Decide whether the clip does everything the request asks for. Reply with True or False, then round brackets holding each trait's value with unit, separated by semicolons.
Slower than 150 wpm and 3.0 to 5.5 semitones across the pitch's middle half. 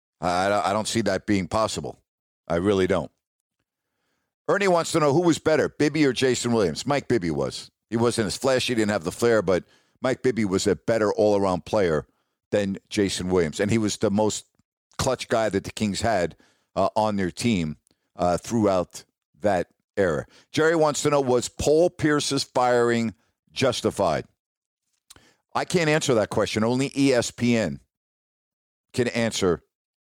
False (160 wpm; 5.0 semitones)